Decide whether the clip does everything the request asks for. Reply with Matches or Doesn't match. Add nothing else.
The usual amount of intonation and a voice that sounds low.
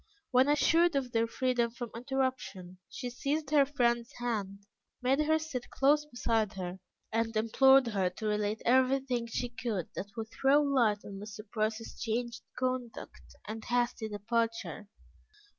Doesn't match